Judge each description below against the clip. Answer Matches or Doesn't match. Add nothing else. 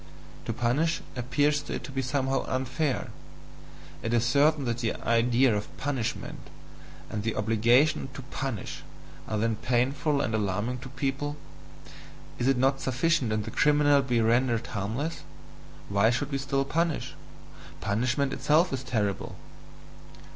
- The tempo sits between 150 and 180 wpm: Doesn't match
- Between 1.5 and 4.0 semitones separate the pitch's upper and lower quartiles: Matches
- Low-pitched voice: Matches